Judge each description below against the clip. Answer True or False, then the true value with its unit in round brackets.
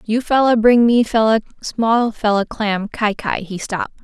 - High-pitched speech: True (220 Hz)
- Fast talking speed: False (165 wpm)